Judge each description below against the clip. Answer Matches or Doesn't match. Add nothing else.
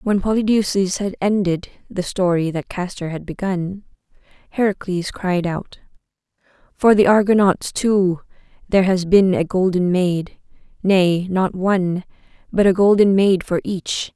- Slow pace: Matches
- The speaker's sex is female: Matches